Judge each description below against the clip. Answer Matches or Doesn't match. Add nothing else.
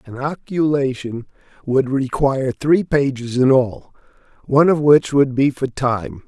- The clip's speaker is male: Matches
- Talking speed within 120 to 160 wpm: Matches